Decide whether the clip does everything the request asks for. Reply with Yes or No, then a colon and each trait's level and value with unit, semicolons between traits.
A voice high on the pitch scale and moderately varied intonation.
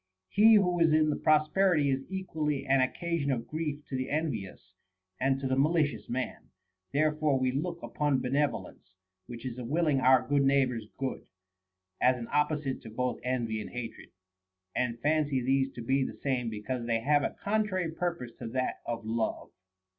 No: low, 135 Hz; average, 3.6 semitones